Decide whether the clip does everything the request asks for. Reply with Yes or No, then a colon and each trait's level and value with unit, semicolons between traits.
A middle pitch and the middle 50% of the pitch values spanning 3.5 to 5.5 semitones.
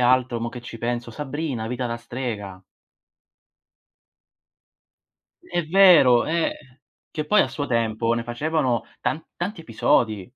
No: low, 125 Hz; average, 4.6 semitones